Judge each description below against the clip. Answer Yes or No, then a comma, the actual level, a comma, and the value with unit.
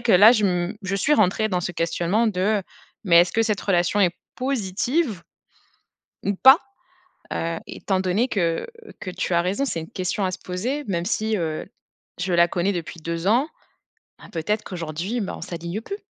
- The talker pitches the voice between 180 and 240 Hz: Yes, high, 190 Hz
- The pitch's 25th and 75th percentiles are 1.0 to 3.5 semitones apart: No, average, 3.9 semitones